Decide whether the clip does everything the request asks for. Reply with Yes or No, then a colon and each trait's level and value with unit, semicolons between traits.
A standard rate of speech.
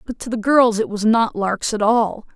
No: fast, 255 wpm